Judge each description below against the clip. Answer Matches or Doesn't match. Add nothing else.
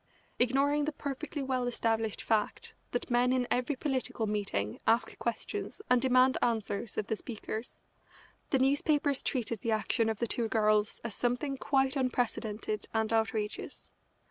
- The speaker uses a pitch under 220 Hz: Doesn't match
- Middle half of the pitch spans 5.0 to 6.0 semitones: Doesn't match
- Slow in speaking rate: Doesn't match